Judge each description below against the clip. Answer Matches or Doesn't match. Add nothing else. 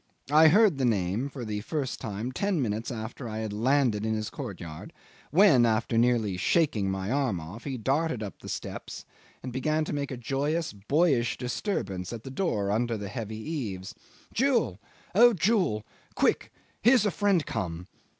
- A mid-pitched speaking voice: Doesn't match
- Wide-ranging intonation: Matches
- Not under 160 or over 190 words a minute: Matches